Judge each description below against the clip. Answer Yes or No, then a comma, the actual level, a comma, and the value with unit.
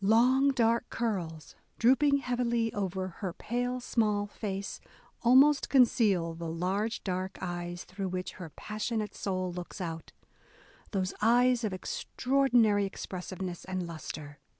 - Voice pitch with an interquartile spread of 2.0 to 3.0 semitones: No, average, 4.7 semitones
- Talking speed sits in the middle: No, slow, 130 wpm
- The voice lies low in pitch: No, high, 205 Hz